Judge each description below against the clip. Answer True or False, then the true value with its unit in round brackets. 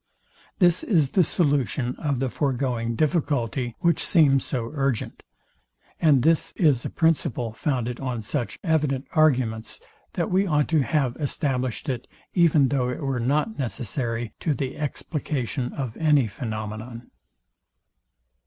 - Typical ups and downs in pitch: True (4.0 semitones)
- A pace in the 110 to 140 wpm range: True (135 wpm)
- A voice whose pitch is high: False (135 Hz)